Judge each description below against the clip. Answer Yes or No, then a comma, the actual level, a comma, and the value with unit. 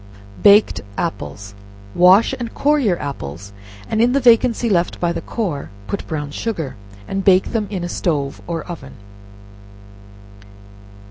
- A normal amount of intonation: No, wide, 6.7 semitones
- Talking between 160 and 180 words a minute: No, average, 140 wpm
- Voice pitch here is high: No, medium, 180 Hz